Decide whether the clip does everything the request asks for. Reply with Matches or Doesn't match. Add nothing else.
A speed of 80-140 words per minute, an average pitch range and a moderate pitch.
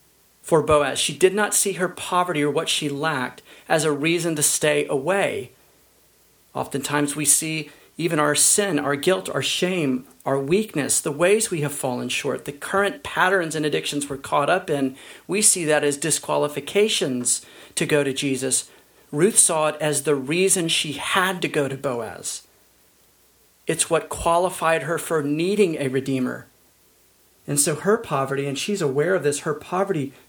Doesn't match